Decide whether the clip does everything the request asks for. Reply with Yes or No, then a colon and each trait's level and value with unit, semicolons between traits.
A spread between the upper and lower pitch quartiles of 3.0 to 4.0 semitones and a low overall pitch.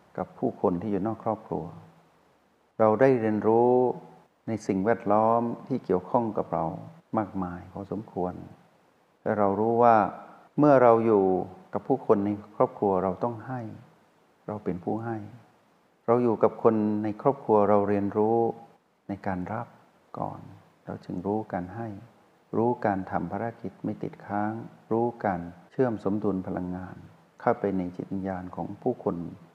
Yes: average, 3.3 semitones; low, 105 Hz